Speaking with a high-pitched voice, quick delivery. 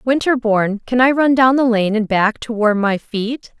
Yes: high, 230 Hz; fast, 215 wpm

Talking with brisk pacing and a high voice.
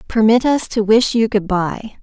Yes: fast, 210 wpm; high, 220 Hz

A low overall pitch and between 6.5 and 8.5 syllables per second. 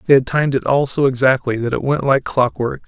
No: low, 130 Hz; 6.0 syllables/s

